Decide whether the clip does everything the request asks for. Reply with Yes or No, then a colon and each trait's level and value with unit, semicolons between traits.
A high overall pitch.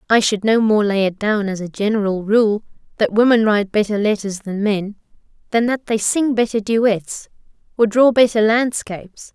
Yes: high, 215 Hz